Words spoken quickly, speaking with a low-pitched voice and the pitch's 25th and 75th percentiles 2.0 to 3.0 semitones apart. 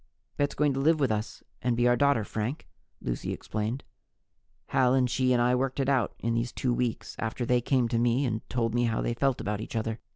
Yes: fast, 230 wpm; low, 120 Hz; narrow, 2.4 semitones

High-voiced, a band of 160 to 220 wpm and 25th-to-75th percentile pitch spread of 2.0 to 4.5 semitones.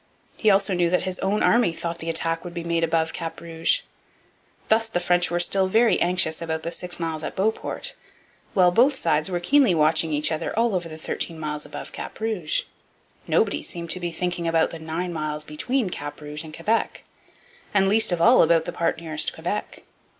No: medium, 170 Hz; average, 200 wpm; average, 3.0 semitones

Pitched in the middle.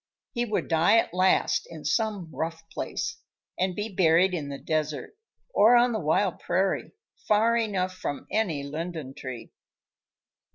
Yes: medium, 180 Hz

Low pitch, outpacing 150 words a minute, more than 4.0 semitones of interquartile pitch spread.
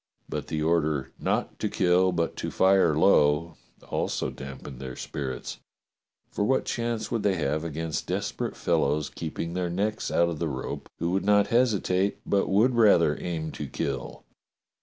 Yes: very low, 85 Hz; average, 160 wpm; average, 4.8 semitones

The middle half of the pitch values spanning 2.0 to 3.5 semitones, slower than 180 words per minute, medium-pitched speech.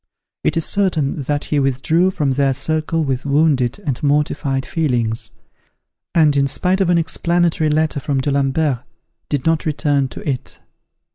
Yes: average, 2.8 semitones; average, 150 wpm; medium, 145 Hz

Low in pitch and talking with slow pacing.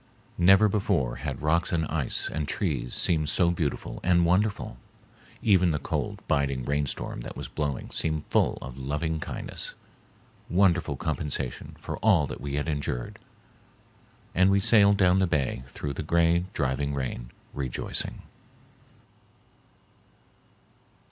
Yes: very low, 80 Hz; slow, 130 wpm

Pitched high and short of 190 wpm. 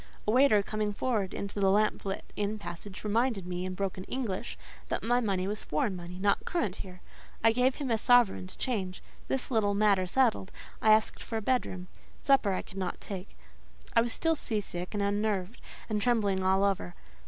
No: high, 205 Hz; average, 195 wpm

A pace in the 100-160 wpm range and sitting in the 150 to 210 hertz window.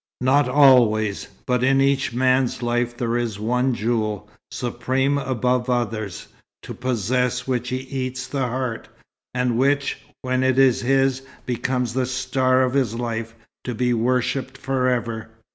No: average, 145 wpm; low, 125 Hz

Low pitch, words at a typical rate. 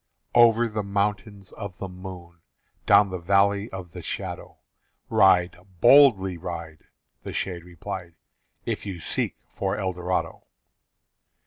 No: very low, 95 Hz; slow, 120 wpm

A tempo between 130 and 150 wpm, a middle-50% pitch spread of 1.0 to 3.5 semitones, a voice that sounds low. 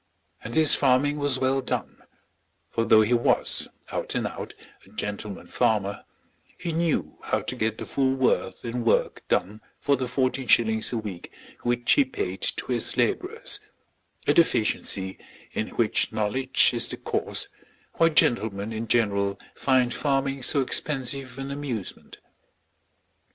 No: average, 145 wpm; average, 4.0 semitones; low, 125 Hz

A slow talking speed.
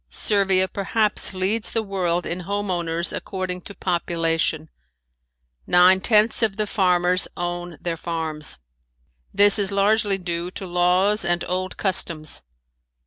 Yes: slow, 130 wpm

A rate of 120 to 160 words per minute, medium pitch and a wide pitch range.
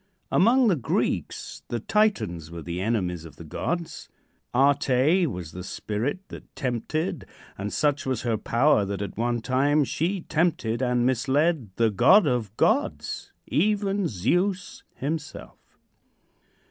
No: slow, 135 wpm; low, 130 Hz; wide, 7.6 semitones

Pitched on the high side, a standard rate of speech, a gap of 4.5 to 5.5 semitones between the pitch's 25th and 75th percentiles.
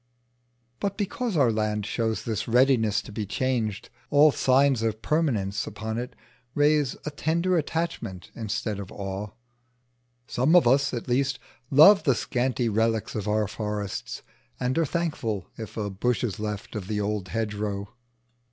No: low, 115 Hz; average, 150 wpm; average, 4.8 semitones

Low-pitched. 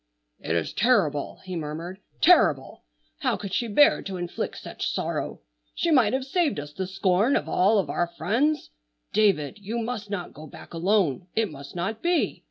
No: high, 195 Hz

